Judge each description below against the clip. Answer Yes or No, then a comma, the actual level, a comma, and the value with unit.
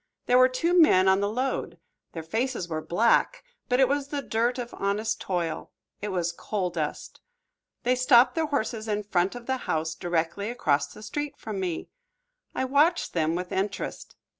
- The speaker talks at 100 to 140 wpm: No, average, 180 wpm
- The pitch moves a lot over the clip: Yes, wide, 6.3 semitones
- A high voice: Yes, high, 215 Hz